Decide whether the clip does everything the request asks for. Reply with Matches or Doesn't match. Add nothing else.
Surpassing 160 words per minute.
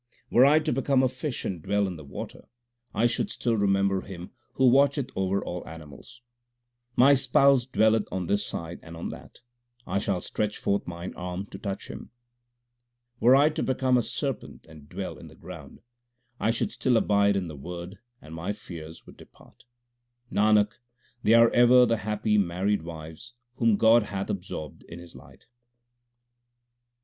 Matches